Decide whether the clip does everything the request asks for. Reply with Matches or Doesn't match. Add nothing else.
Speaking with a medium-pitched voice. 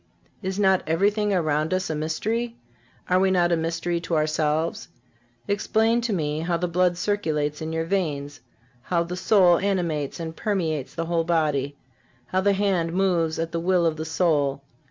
Matches